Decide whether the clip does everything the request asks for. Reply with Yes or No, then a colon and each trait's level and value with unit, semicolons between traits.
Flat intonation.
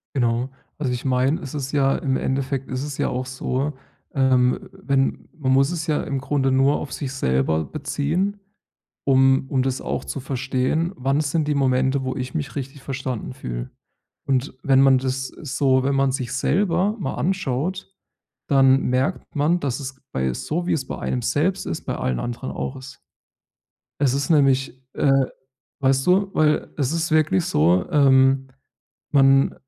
Yes: narrow, 2.2 semitones